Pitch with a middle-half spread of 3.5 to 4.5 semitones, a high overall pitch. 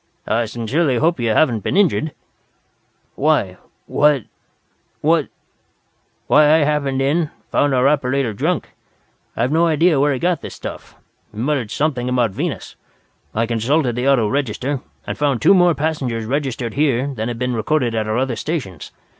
No: average, 4.2 semitones; low, 135 Hz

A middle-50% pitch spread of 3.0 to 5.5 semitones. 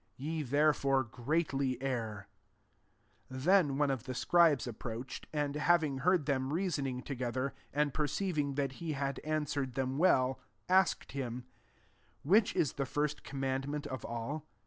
No: narrow, 2.6 semitones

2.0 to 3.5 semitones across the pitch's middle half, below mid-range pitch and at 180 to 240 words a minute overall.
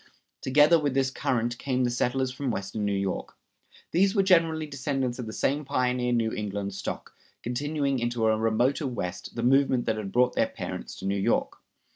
No: average, 3.9 semitones; low, 125 Hz; average, 185 wpm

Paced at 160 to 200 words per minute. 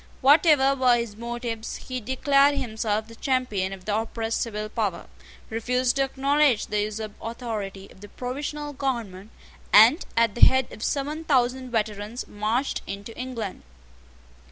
No: average, 145 wpm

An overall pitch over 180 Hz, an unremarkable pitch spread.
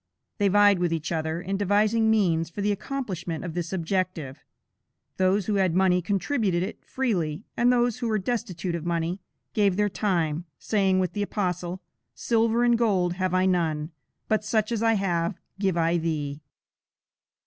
Yes: high, 190 Hz; average, 3.5 semitones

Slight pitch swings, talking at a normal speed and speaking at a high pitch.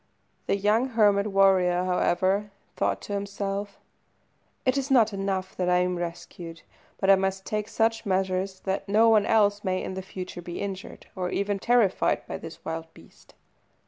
Yes: narrow, 2.1 semitones; average, 165 wpm; high, 195 Hz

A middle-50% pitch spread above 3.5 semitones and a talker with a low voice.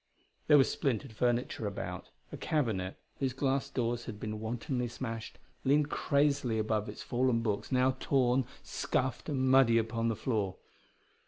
No: average, 3.0 semitones; low, 120 Hz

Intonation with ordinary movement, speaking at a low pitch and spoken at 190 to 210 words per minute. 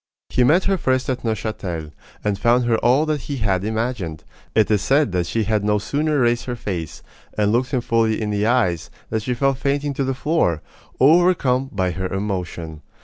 Yes: average, 4.8 semitones; low, 115 Hz; average, 200 wpm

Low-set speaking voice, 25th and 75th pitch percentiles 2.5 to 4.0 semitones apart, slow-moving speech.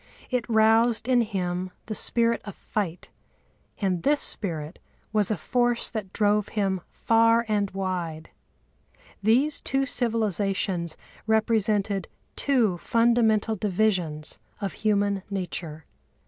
No: high, 210 Hz; average, 3.4 semitones; slow, 110 wpm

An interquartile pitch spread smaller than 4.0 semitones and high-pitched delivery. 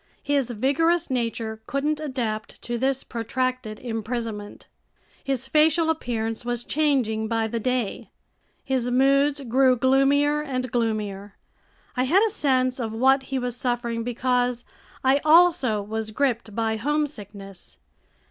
Yes: average, 3.5 semitones; very high, 250 Hz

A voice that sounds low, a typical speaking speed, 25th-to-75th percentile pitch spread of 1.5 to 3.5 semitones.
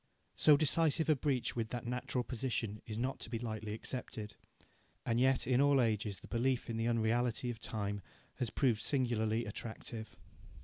Yes: low, 120 Hz; average, 170 wpm; average, 2.7 semitones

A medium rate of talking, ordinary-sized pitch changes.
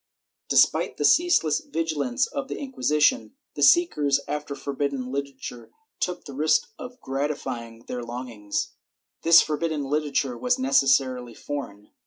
No: slow, 130 wpm; average, 4.4 semitones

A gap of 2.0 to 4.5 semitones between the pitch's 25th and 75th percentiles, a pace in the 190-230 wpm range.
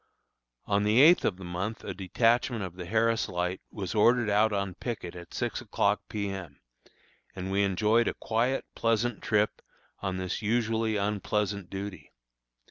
No: average, 3.1 semitones; average, 160 wpm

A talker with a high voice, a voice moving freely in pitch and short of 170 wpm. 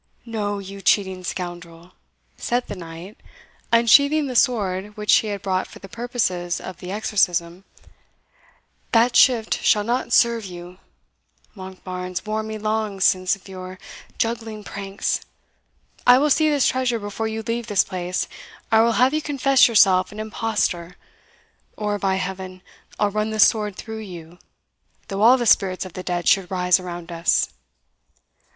No: high, 205 Hz; average, 3.6 semitones; average, 155 wpm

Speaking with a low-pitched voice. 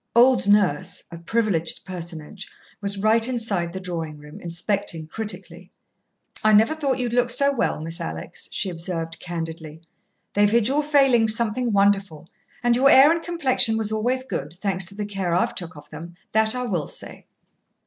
No: high, 205 Hz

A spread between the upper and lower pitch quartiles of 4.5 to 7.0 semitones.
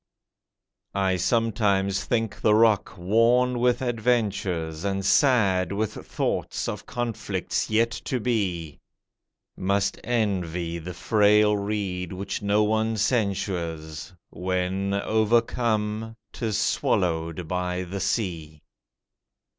No: average, 3.5 semitones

